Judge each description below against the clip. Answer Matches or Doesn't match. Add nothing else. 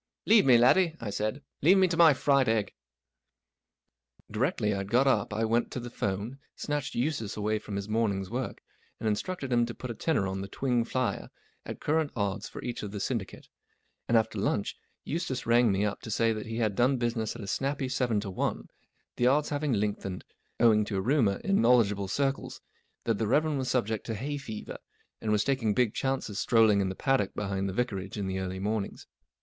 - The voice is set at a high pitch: Doesn't match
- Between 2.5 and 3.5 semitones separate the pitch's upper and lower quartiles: Doesn't match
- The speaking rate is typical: Doesn't match